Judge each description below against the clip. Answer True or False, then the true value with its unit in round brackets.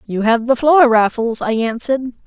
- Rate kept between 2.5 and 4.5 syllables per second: False (4.9 syllables/s)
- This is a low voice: False (240 Hz)